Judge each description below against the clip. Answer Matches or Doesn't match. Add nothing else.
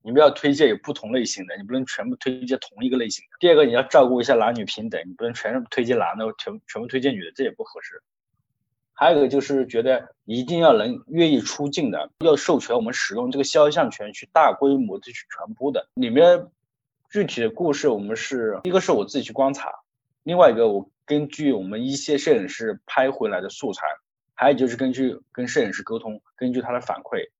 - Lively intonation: Doesn't match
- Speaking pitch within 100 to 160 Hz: Matches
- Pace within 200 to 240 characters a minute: Doesn't match